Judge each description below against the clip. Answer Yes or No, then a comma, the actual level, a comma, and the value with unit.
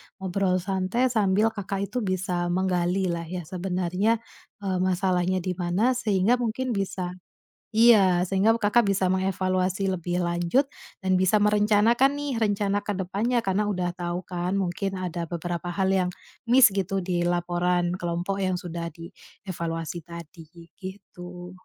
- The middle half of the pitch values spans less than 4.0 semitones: Yes, narrow, 2.4 semitones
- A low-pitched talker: No, medium, 185 Hz